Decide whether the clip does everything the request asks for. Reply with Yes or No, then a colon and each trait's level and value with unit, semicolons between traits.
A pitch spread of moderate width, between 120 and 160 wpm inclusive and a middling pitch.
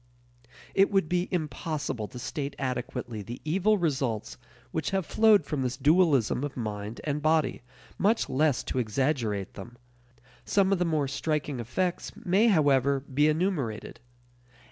No: wide, 5.7 semitones; average, 145 wpm; medium, 145 Hz